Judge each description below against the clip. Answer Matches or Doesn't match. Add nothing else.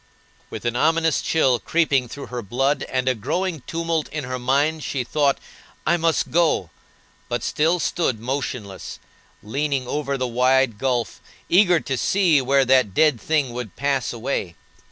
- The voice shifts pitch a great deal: Doesn't match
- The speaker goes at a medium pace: Matches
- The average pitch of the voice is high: Doesn't match